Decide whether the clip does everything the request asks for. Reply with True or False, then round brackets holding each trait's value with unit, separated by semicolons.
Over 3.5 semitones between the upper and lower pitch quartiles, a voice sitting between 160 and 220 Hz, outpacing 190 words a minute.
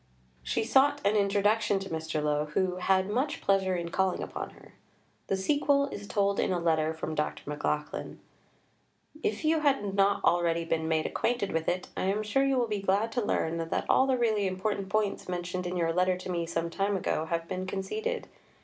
True (4.0 semitones; 190 Hz; 200 wpm)